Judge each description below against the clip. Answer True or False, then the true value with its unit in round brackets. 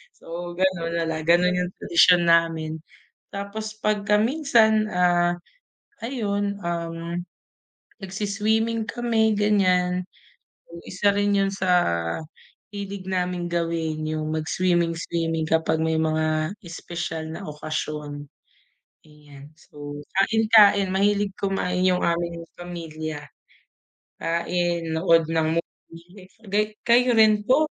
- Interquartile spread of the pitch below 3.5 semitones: False (3.8 semitones)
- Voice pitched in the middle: True (175 Hz)